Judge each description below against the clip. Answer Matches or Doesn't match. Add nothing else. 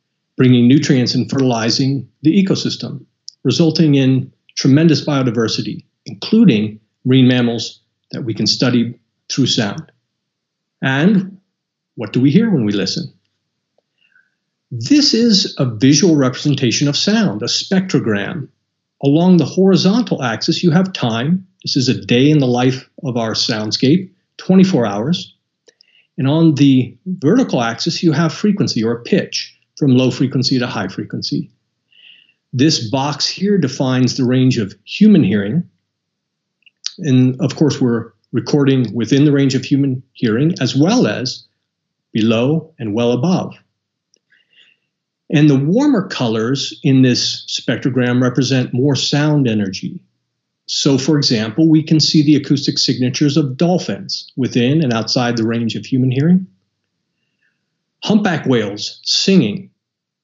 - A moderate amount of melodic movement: Matches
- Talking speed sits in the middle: Doesn't match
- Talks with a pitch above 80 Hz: Matches